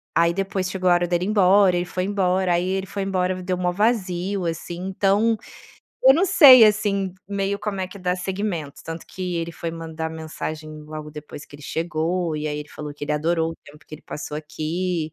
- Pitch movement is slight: No, average, 3.2 semitones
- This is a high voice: No, medium, 180 Hz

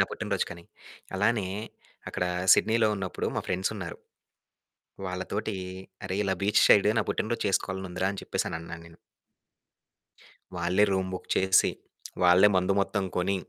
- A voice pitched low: Yes, very low, 95 Hz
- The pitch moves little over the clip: Yes, narrow, 2.0 semitones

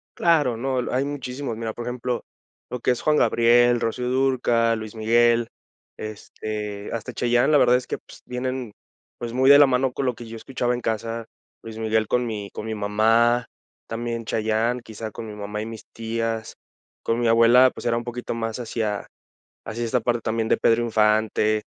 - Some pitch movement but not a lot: No, narrow, 1.9 semitones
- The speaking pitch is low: Yes, low, 115 Hz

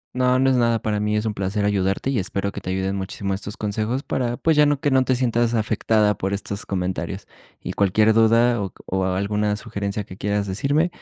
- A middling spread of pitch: Yes, average, 3.3 semitones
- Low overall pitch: Yes, low, 105 Hz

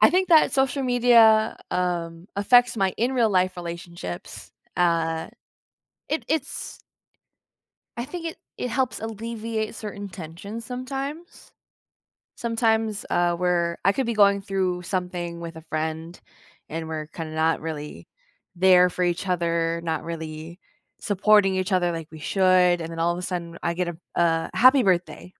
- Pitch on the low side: No, medium, 180 Hz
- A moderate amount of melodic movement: Yes, average, 4.9 semitones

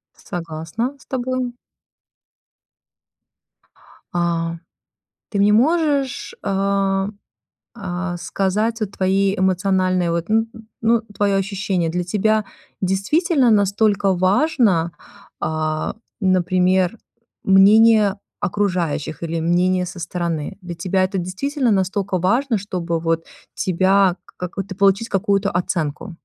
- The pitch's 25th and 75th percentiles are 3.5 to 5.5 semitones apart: No, average, 3.1 semitones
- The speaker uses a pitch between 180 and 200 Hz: Yes, high, 190 Hz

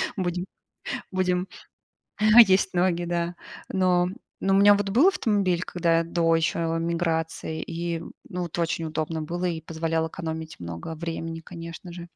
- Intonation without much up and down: Yes, narrow, 1.9 semitones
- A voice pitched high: No, medium, 170 Hz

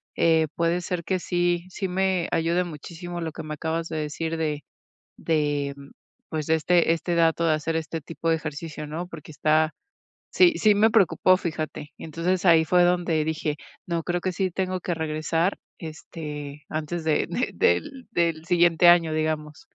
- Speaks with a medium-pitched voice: Yes, medium, 165 Hz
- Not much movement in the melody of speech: Yes, narrow, 2.1 semitones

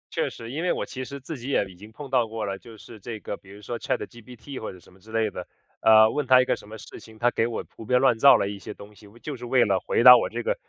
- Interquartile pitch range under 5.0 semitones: Yes, average, 3.2 semitones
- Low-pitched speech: Yes, low, 115 Hz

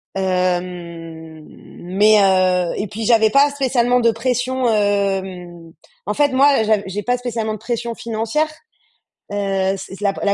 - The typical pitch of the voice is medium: No, high, 210 Hz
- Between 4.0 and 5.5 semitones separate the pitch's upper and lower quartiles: Yes, average, 4.4 semitones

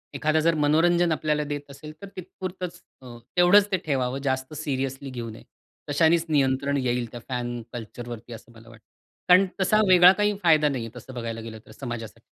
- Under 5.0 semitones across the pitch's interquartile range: No, wide, 5.6 semitones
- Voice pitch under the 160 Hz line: Yes, medium, 140 Hz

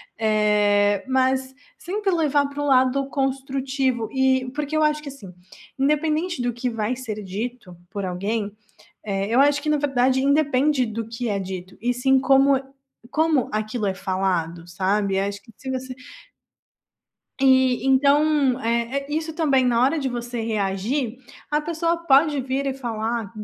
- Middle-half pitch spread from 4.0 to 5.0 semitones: Yes, average, 4.6 semitones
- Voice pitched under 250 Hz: No, very high, 260 Hz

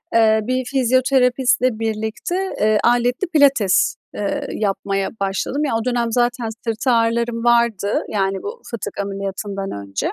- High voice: Yes, high, 230 Hz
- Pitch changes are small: No, average, 3.6 semitones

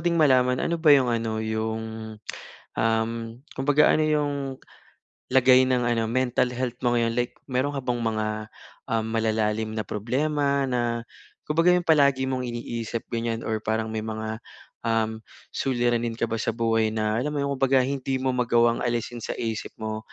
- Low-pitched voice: Yes, low, 120 Hz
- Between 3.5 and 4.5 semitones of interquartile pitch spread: No, average, 2.8 semitones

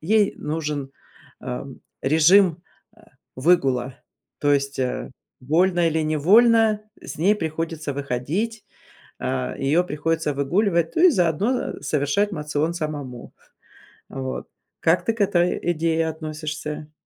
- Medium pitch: Yes, medium, 160 Hz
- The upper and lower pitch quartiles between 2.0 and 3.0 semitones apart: No, average, 3.7 semitones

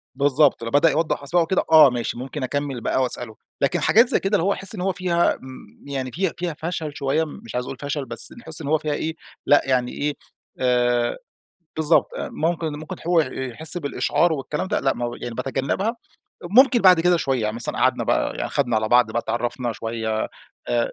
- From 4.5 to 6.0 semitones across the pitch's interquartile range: Yes, average, 5.1 semitones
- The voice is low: No, medium, 145 Hz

